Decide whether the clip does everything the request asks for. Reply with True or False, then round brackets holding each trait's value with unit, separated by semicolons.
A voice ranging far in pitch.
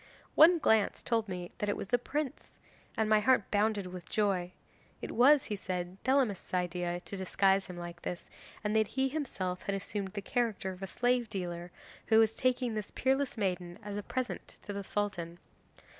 False (4.5 semitones)